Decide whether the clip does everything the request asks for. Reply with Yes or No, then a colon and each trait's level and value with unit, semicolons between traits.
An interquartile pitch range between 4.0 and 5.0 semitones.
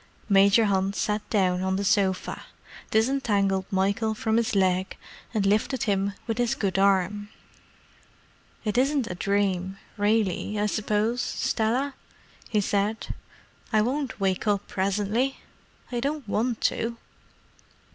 No: narrow, 2.6 semitones